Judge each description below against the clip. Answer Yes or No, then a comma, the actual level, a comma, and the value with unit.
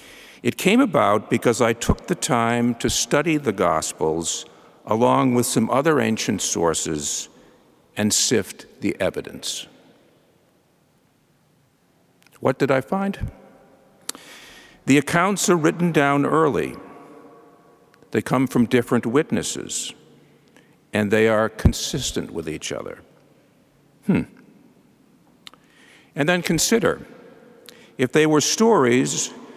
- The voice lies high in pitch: No, medium, 140 Hz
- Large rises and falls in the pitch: Yes, wide, 6.9 semitones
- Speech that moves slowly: Yes, slow, 105 wpm